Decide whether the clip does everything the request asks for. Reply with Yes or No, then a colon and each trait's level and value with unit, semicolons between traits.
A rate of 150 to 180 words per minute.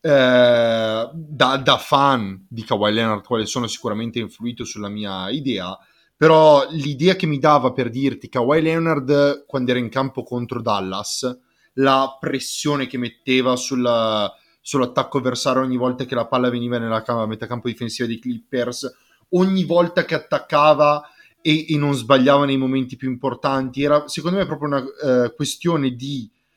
Yes: average, 155 wpm